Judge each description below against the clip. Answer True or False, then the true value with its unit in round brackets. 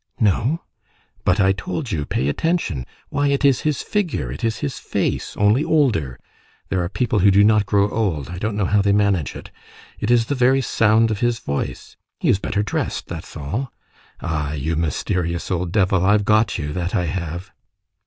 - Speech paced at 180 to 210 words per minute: True (190 wpm)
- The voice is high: False (100 Hz)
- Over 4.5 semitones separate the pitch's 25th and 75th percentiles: True (5.0 semitones)